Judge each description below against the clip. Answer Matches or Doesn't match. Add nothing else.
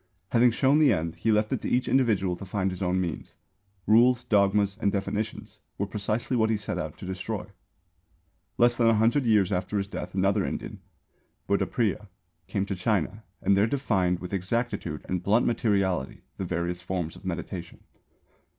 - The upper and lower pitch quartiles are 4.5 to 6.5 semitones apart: Doesn't match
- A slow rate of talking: Doesn't match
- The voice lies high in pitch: Doesn't match